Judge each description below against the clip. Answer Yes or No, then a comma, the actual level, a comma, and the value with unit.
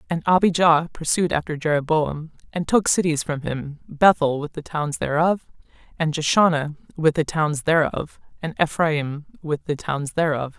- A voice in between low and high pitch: Yes, medium, 155 Hz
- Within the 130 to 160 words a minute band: Yes, average, 155 wpm